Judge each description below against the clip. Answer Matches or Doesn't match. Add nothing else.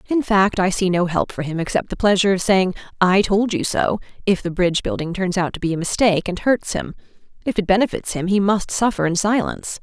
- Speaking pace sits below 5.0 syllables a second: Doesn't match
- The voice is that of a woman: Matches